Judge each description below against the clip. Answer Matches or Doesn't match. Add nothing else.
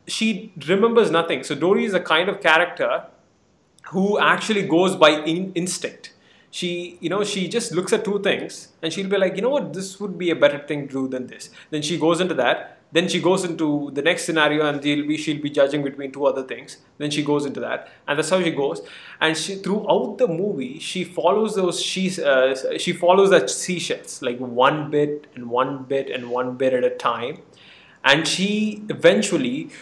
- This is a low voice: Doesn't match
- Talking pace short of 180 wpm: Doesn't match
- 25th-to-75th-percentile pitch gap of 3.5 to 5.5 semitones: Matches